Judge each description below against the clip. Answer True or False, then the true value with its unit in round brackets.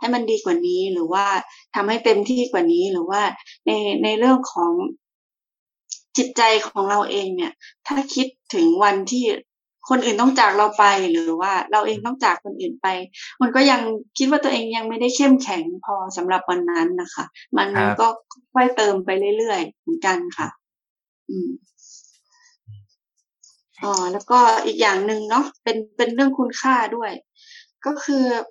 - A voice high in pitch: True (250 Hz)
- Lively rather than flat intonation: True (7.9 semitones)